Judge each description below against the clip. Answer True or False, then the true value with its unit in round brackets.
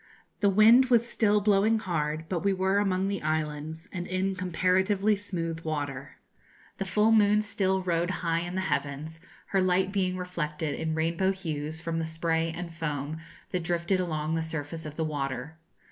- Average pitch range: True (3.2 semitones)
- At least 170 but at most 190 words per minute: True (175 wpm)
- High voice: False (170 Hz)